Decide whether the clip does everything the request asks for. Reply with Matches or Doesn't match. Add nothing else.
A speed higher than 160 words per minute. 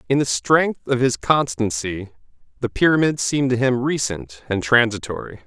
Doesn't match